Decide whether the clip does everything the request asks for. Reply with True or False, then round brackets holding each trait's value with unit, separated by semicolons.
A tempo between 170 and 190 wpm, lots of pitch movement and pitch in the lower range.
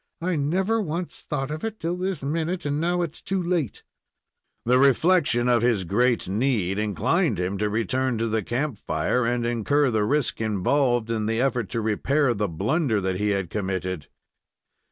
True (175 wpm; 6.3 semitones; 125 Hz)